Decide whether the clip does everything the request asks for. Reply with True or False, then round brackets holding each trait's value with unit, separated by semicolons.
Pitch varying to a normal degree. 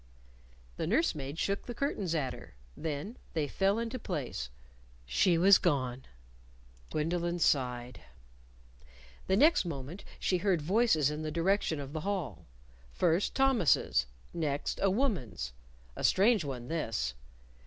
False (6.0 semitones)